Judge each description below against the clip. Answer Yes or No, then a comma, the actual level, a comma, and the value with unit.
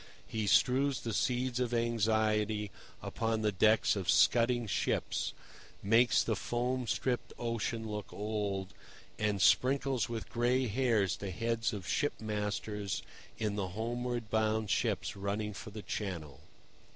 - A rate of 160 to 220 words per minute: No, slow, 135 wpm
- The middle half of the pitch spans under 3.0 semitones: Yes, narrow, 2.5 semitones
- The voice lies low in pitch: Yes, low, 110 Hz